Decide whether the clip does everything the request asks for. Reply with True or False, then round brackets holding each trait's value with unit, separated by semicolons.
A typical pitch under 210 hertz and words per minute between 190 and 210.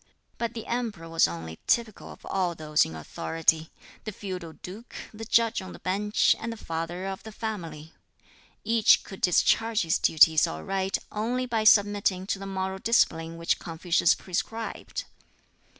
False (190 Hz; 155 wpm)